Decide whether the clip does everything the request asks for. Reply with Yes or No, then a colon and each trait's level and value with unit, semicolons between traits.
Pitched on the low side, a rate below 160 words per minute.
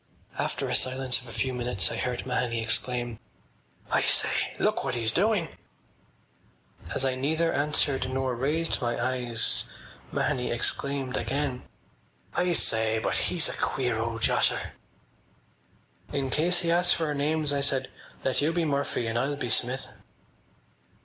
Yes: low, 130 Hz; average, 150 wpm